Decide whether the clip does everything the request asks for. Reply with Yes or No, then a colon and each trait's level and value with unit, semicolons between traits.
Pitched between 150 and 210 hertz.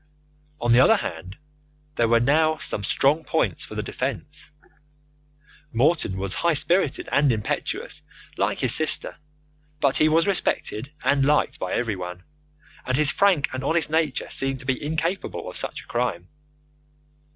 No: low, 135 Hz